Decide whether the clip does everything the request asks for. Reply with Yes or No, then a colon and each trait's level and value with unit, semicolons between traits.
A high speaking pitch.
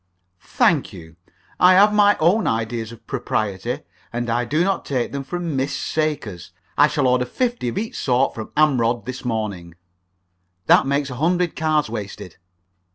No: low, 130 Hz